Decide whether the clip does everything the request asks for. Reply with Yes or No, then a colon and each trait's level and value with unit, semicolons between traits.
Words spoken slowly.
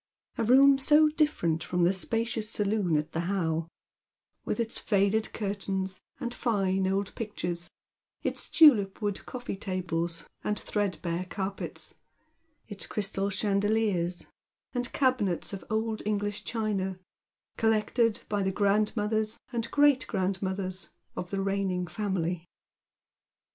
Yes: slow, 115 wpm